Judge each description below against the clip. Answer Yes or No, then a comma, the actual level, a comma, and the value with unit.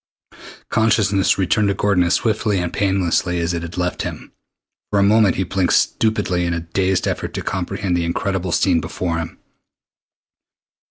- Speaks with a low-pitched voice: Yes, very low, 95 Hz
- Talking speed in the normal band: Yes, average, 165 wpm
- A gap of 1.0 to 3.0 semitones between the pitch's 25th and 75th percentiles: Yes, narrow, 2.5 semitones